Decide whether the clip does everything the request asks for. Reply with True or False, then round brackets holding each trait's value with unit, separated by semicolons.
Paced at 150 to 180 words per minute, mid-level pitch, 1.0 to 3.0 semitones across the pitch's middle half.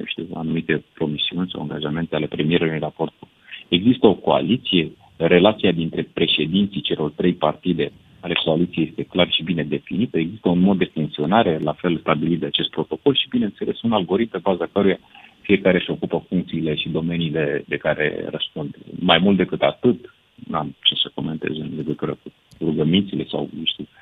False (165 wpm; 85 Hz; 2.7 semitones)